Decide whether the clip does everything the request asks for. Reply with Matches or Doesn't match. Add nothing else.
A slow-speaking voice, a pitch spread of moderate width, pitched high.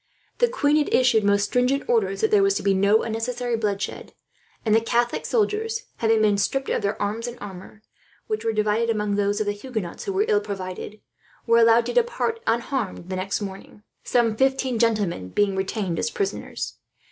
Doesn't match